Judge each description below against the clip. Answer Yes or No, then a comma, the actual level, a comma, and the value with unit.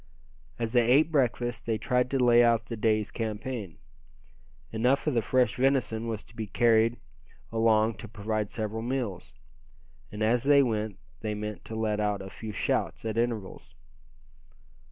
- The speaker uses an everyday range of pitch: No, narrow, 2.2 semitones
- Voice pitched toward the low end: Yes, low, 115 Hz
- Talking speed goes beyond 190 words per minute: No, average, 160 wpm